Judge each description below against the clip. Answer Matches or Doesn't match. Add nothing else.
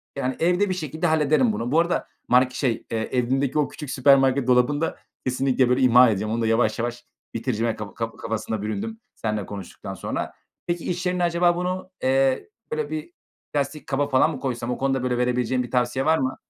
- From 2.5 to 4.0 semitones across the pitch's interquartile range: Doesn't match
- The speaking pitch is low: Matches